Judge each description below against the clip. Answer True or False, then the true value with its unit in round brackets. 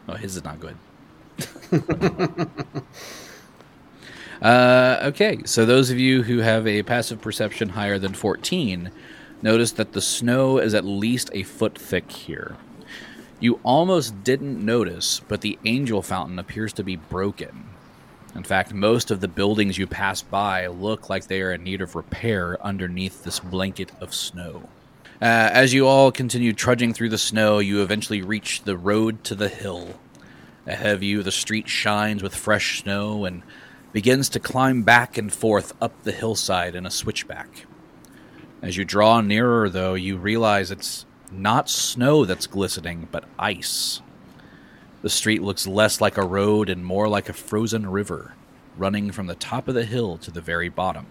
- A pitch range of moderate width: True (3.4 semitones)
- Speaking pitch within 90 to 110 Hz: True (105 Hz)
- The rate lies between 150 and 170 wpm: True (165 wpm)